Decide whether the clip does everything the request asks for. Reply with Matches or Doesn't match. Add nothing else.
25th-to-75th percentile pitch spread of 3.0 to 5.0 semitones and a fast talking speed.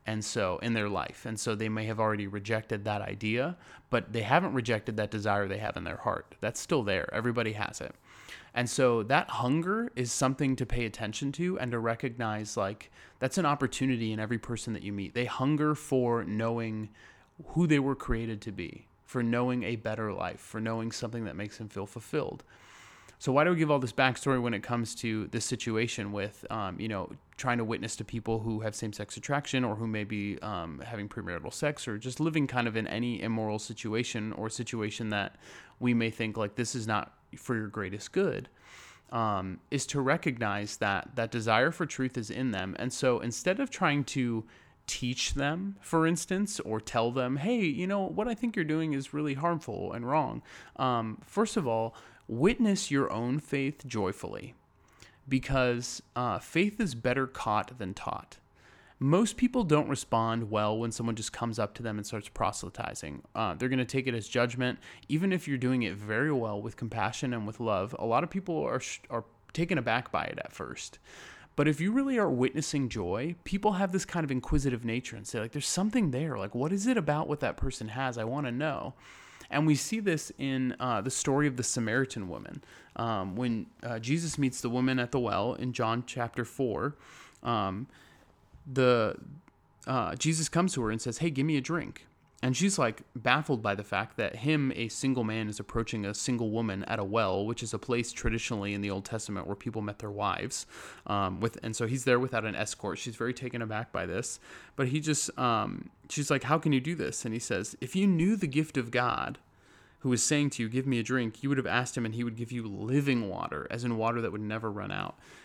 Matches